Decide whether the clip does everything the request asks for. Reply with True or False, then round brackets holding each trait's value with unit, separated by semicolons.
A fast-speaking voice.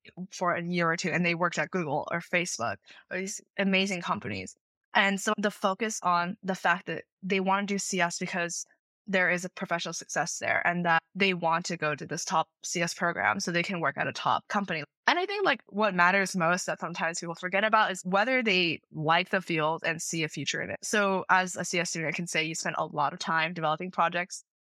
True (230 wpm)